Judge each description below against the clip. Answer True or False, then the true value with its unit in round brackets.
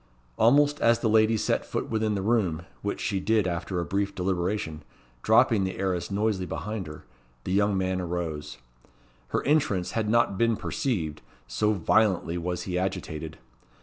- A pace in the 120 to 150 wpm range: False (160 wpm)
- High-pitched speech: False (95 Hz)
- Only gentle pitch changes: False (3.7 semitones)